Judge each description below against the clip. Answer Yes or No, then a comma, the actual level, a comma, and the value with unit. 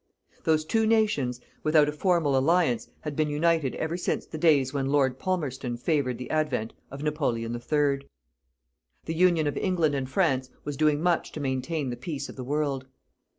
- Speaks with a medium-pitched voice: Yes, medium, 145 Hz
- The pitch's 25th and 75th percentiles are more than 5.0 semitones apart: No, average, 3.3 semitones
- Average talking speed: Yes, average, 175 wpm